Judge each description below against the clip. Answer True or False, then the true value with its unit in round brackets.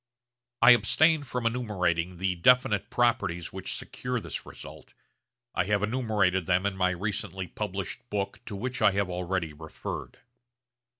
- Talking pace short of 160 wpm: True (140 wpm)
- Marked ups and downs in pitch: False (4.6 semitones)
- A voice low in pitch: True (100 Hz)